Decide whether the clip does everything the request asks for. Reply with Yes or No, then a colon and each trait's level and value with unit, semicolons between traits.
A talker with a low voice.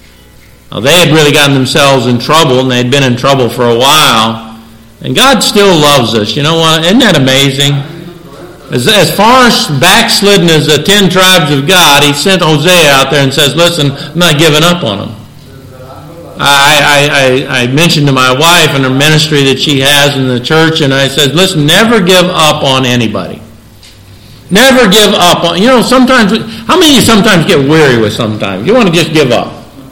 No: medium, 145 Hz